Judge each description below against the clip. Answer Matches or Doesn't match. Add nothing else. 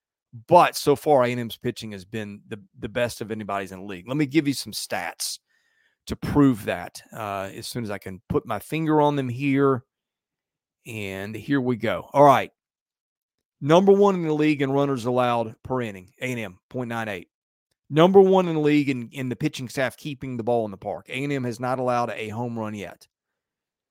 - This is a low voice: Matches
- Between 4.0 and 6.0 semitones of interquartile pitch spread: Matches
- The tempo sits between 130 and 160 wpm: Doesn't match